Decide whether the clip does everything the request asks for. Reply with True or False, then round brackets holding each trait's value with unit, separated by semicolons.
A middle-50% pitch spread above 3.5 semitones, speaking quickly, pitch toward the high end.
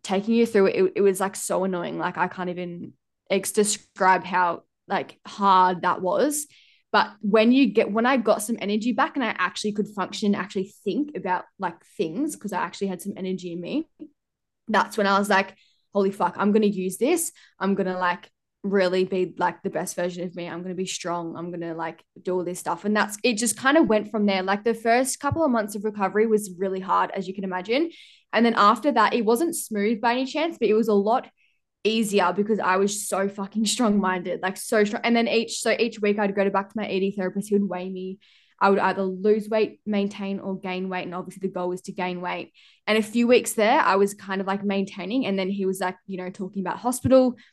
False (3.0 semitones; 235 wpm; 200 Hz)